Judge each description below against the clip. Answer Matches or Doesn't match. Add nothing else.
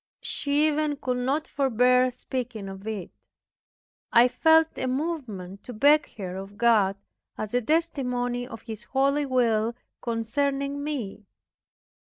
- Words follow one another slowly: Matches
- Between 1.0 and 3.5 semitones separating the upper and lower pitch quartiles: Doesn't match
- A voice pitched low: Doesn't match